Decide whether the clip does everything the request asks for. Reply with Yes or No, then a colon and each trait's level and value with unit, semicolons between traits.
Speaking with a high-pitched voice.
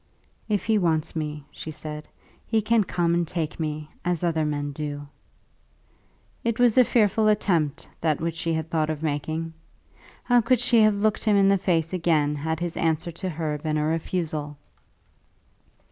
No: medium, 165 Hz